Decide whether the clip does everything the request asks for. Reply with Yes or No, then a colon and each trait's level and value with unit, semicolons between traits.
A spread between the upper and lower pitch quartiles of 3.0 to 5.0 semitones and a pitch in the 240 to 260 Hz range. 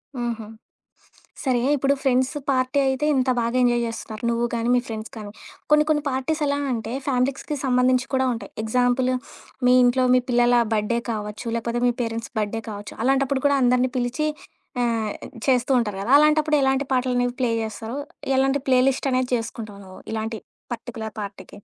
No: narrow, 2.6 semitones; high, 245 Hz